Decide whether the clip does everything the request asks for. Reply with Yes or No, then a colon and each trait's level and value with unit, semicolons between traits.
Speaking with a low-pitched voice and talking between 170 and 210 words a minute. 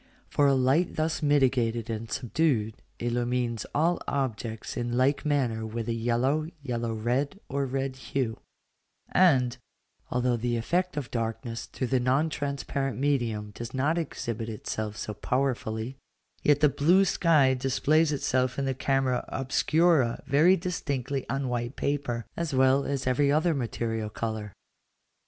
No: low, 130 Hz; average, 140 wpm